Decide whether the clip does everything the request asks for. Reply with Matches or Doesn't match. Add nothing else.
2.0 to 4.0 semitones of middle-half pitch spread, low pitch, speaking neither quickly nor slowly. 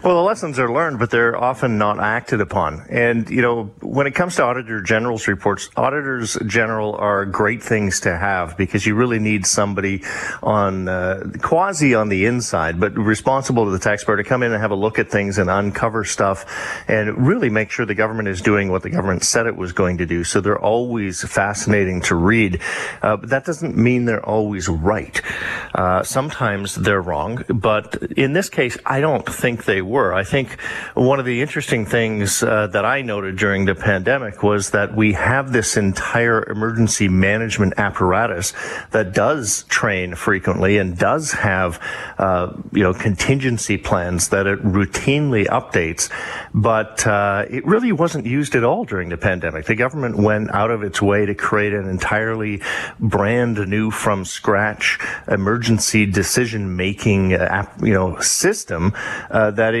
Matches